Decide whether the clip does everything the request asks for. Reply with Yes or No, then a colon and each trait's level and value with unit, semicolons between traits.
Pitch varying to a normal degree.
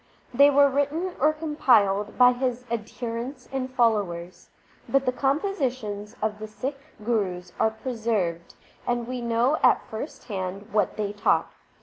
Yes: average, 4.3 semitones